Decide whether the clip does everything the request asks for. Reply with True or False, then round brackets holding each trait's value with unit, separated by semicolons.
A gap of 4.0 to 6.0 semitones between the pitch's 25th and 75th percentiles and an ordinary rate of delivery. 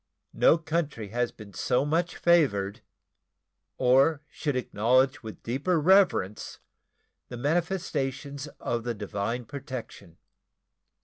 False (5.2 semitones; 105 wpm)